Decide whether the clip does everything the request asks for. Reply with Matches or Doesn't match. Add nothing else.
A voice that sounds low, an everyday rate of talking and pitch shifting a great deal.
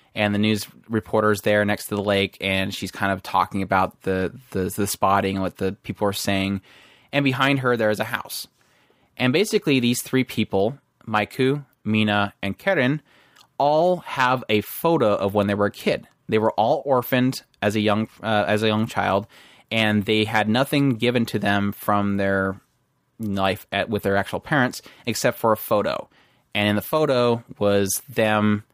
Doesn't match